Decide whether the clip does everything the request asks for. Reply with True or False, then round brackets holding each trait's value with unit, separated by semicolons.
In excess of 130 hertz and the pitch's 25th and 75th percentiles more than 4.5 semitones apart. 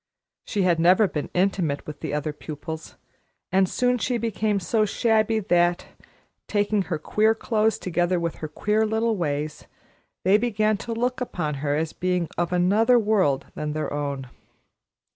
True (185 Hz; 5.6 semitones)